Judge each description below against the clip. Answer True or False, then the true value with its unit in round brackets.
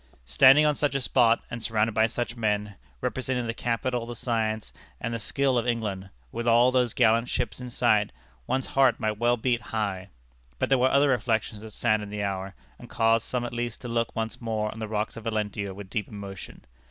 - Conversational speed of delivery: False (210 wpm)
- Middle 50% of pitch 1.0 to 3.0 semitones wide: True (2.4 semitones)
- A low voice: True (115 Hz)